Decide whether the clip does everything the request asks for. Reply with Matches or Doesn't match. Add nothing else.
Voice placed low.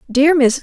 Doesn't match